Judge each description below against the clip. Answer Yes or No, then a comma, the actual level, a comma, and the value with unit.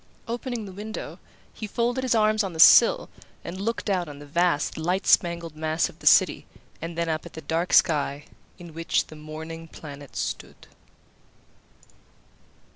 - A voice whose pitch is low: No, medium, 170 Hz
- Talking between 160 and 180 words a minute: Yes, average, 165 wpm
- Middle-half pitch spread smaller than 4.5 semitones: No, average, 4.8 semitones